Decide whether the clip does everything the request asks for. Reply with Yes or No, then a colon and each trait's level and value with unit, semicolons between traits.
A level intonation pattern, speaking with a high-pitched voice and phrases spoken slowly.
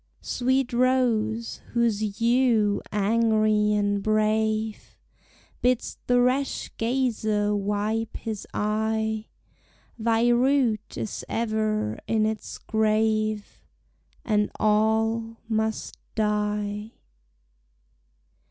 Yes: narrow, 1.5 semitones; high, 220 Hz; slow, 80 wpm